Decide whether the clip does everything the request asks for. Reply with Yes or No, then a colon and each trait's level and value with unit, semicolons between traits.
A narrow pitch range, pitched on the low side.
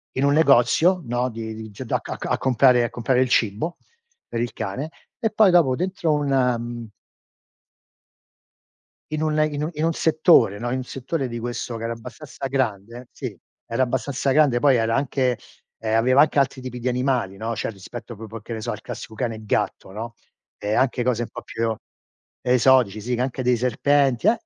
No: average, 3.2 semitones; low, 125 Hz